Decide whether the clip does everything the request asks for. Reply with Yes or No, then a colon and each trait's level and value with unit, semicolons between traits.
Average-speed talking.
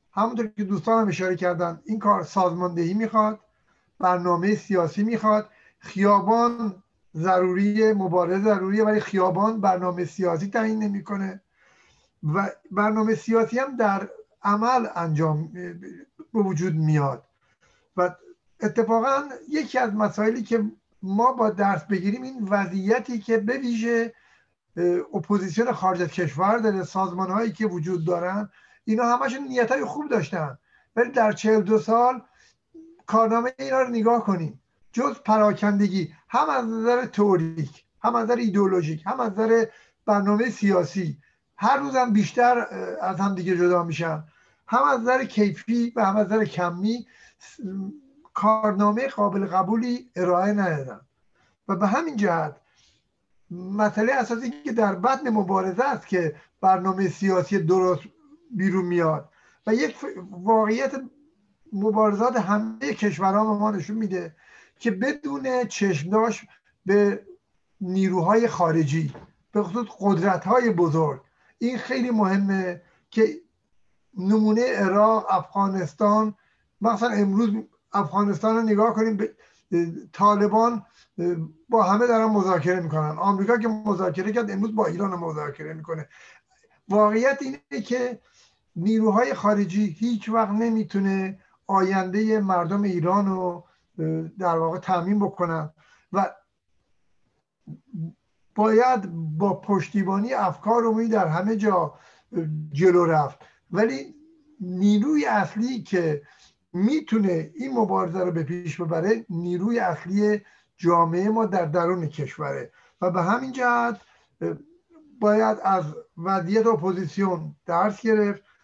Yes: average, 120 wpm